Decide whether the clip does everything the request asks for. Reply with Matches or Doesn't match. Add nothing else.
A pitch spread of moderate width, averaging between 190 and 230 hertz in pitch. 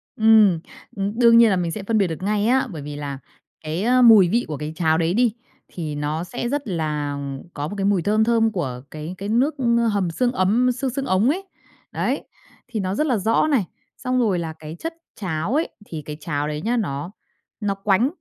Doesn't match